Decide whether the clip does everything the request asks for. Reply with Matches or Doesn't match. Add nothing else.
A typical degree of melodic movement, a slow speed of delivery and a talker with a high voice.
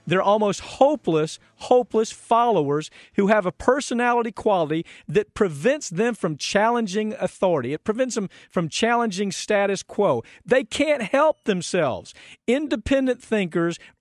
Matches